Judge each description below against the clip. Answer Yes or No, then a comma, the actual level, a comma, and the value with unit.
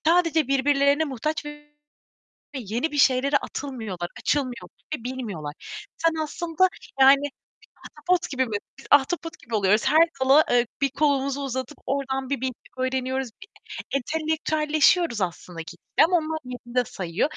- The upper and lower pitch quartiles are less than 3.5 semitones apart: No, average, 3.8 semitones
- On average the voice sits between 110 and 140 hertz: No, very high, 275 Hz